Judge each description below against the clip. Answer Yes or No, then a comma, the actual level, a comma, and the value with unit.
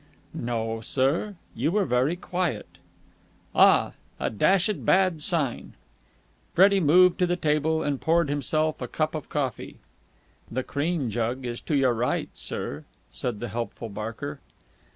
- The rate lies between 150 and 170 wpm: No, average, 140 wpm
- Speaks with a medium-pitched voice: Yes, medium, 145 Hz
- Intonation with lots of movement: Yes, wide, 5.9 semitones